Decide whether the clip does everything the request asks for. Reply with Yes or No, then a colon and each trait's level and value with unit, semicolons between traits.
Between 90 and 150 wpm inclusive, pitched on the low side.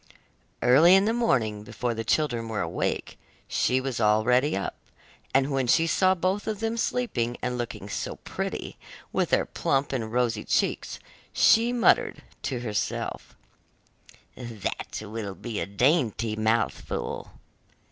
Yes: slow, 135 wpm; low, 125 Hz